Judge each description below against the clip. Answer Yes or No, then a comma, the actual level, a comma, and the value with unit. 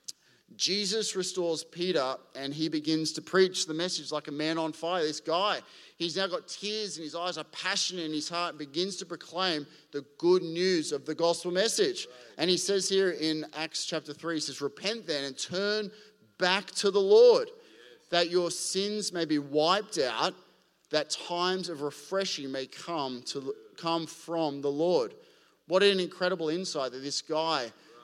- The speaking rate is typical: Yes, average, 180 wpm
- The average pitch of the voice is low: No, medium, 170 Hz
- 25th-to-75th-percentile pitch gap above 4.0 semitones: No, average, 3.7 semitones